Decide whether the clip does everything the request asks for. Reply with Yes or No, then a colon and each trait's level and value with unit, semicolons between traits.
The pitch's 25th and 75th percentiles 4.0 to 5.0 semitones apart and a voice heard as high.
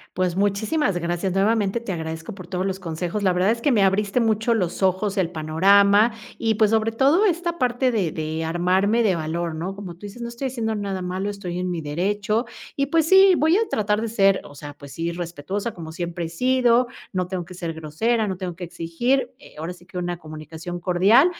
Yes: average, 4.5 semitones; high, 195 Hz